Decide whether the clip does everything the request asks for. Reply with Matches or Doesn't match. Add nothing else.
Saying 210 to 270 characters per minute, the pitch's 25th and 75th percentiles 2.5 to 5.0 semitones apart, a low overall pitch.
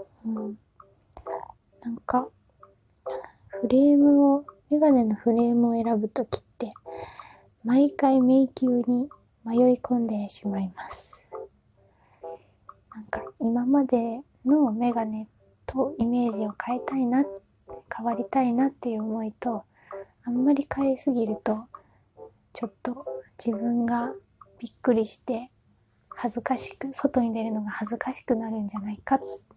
Doesn't match